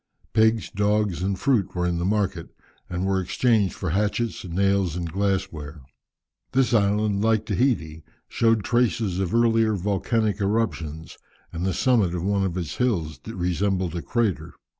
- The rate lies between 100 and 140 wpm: No, average, 155 wpm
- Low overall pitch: Yes, low, 100 Hz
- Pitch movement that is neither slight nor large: Yes, average, 3.8 semitones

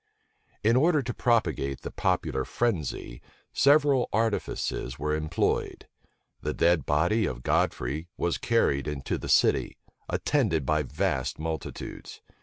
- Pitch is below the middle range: Yes, very low, 80 Hz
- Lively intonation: Yes, wide, 8.2 semitones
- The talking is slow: Yes, slow, 125 wpm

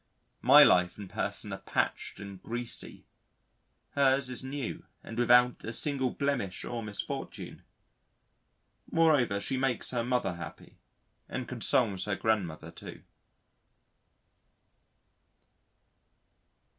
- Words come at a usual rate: No, slow, 105 wpm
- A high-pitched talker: No, low, 120 Hz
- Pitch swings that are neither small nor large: Yes, average, 4.6 semitones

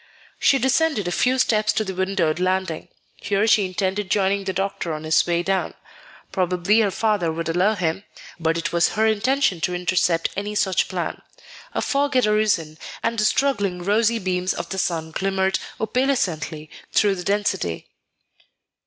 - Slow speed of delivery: No, average, 165 wpm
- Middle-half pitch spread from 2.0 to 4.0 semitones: Yes, average, 3.5 semitones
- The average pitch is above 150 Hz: Yes, high, 190 Hz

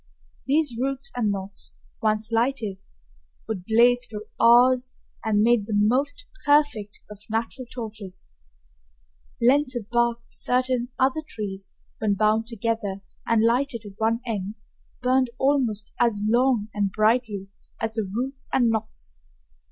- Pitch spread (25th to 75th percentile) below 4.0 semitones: Yes, average, 3.2 semitones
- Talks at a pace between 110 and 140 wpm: Yes, slow, 135 wpm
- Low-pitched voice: No, high, 230 Hz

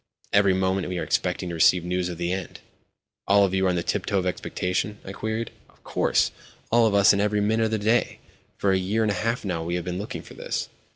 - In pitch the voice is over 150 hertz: No, very low, 95 Hz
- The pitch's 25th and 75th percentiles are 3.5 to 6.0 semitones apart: No, narrow, 2.6 semitones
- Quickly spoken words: Yes, fast, 245 wpm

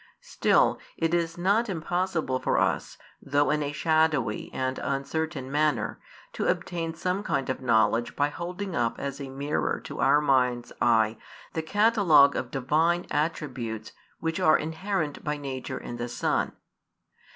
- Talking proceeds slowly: No, average, 150 wpm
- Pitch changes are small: No, average, 4.4 semitones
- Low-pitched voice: No, medium, 150 Hz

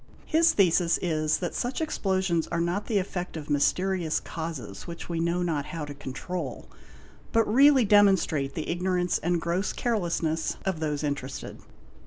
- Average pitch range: Yes, average, 3.5 semitones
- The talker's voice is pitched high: No, medium, 170 Hz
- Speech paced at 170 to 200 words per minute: No, average, 155 wpm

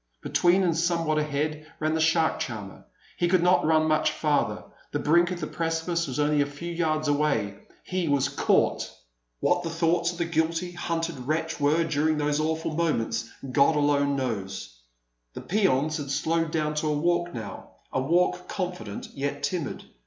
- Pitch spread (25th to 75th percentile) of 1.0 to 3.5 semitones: Yes, average, 2.8 semitones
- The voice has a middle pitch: Yes, medium, 155 Hz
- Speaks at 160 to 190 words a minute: Yes, average, 175 wpm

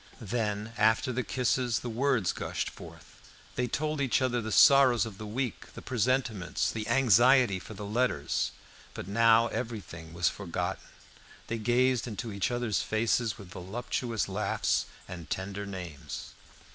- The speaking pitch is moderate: No, low, 115 Hz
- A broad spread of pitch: No, average, 3.8 semitones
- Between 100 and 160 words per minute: Yes, average, 145 wpm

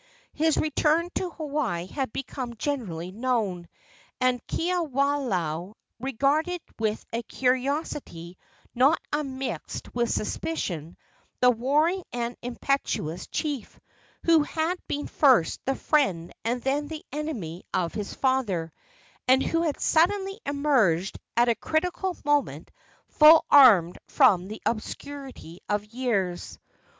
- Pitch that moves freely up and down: Yes, wide, 6.1 semitones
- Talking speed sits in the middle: No, slow, 115 wpm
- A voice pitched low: No, very high, 260 Hz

